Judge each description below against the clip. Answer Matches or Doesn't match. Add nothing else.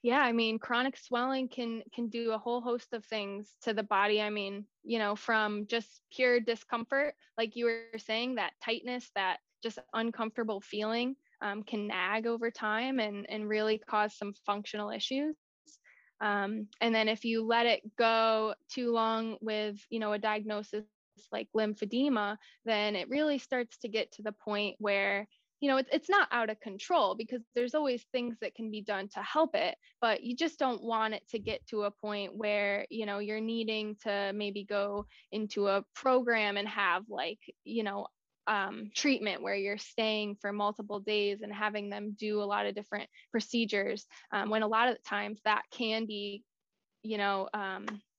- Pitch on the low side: Doesn't match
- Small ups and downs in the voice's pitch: Matches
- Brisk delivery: Doesn't match